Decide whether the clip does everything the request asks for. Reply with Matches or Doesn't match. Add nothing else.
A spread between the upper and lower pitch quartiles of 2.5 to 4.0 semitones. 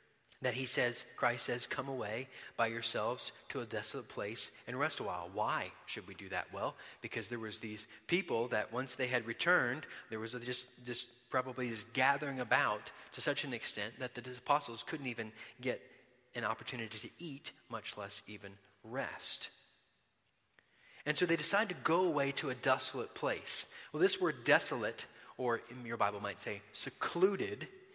Matches